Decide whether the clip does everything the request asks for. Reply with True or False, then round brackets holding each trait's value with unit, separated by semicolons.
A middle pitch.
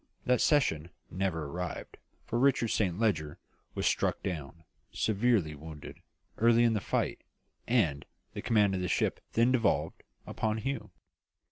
False (100 Hz)